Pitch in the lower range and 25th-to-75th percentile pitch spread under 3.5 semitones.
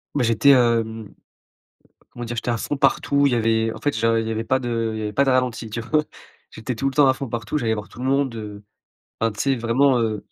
Yes: low, 115 Hz; average, 2.9 semitones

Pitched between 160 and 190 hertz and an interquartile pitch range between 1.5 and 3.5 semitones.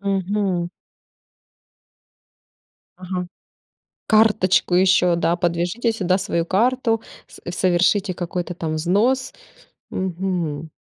Yes: medium, 185 Hz; average, 2.7 semitones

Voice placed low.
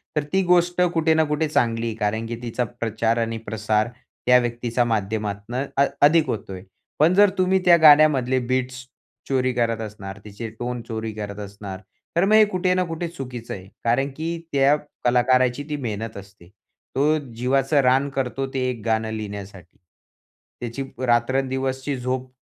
Yes: low, 125 Hz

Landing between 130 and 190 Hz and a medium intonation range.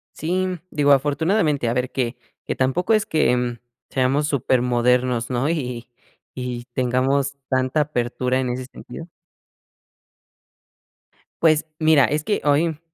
Yes: low, 135 Hz; average, 3.5 semitones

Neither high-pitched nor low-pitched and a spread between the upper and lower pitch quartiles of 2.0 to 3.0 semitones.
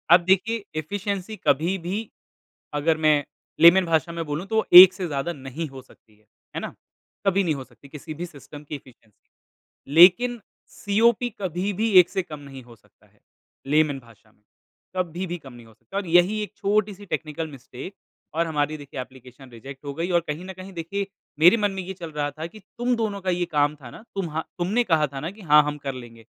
No: medium, 165 Hz; average, 5.0 semitones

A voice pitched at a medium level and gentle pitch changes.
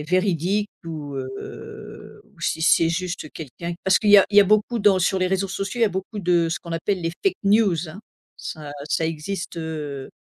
No: medium, 175 Hz; average, 3.5 semitones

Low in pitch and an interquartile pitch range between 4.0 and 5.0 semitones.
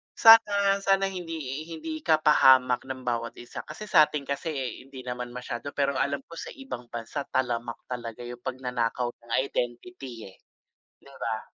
Yes: low, 130 Hz; average, 4.5 semitones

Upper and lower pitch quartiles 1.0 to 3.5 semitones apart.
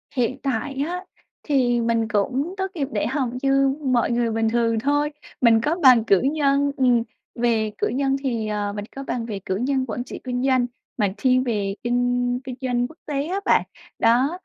Yes: average, 3.0 semitones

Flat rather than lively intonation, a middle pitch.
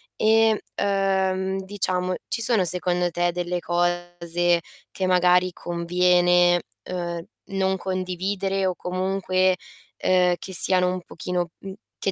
Yes: narrow, 1.4 semitones; medium, 180 Hz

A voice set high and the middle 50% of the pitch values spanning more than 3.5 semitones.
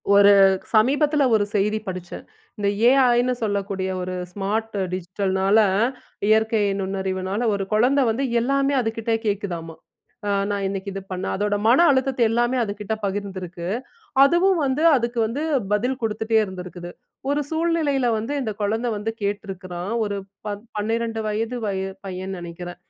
Yes: high, 210 Hz; average, 3.9 semitones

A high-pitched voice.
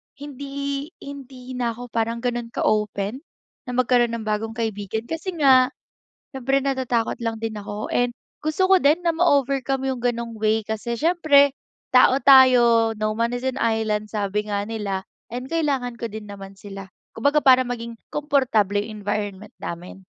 Yes: high, 235 Hz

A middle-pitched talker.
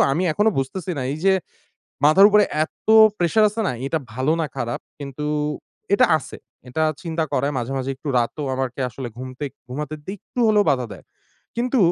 Yes: medium, 150 Hz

